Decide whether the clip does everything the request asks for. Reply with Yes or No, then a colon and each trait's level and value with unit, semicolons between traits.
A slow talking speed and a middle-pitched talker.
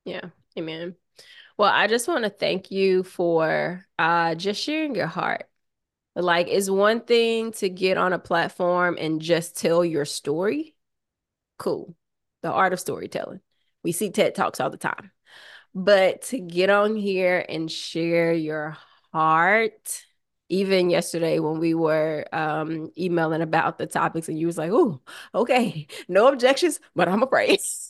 No: average, 155 wpm; medium, 180 Hz